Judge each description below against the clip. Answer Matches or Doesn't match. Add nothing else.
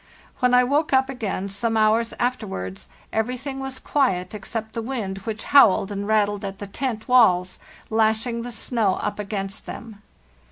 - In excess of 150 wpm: Matches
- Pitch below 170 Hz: Doesn't match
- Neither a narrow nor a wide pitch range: Matches